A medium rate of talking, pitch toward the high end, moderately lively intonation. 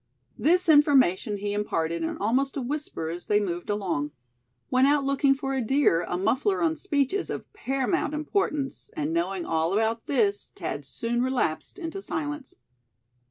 No: average, 160 wpm; very high, 255 Hz; wide, 7.4 semitones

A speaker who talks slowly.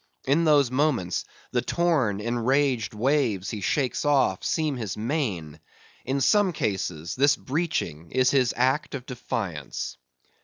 Yes: slow, 130 wpm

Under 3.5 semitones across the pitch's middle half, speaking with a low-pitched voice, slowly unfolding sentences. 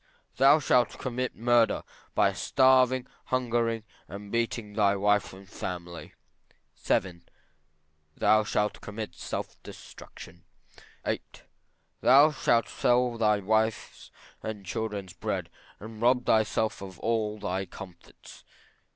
Yes: average, 3.0 semitones; low, 110 Hz; slow, 110 wpm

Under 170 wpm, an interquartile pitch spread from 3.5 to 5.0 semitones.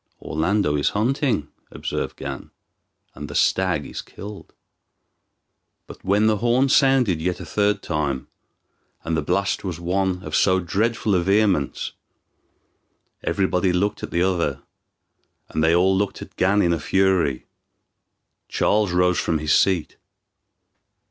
Yes: average, 140 wpm; average, 4.0 semitones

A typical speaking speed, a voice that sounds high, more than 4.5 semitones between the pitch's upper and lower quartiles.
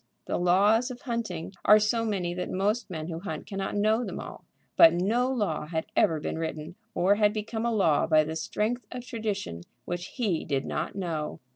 Yes: average, 195 wpm; high, 195 Hz; average, 5.2 semitones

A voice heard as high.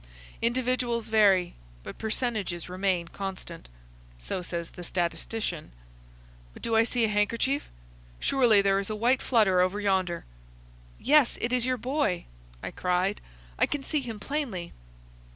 Yes: high, 210 Hz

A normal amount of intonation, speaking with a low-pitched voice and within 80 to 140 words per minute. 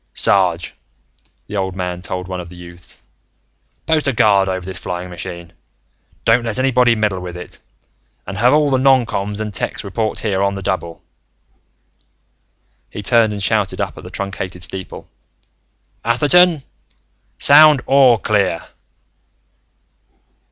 Yes: average, 4.7 semitones; low, 100 Hz; slow, 135 wpm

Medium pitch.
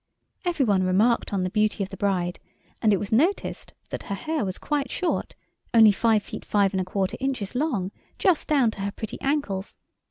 No: high, 210 Hz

